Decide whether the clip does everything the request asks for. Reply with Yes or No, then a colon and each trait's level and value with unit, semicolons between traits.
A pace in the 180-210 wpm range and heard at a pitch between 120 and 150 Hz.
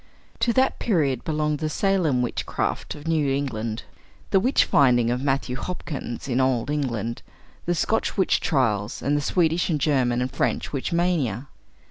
No: average, 160 wpm; medium, 140 Hz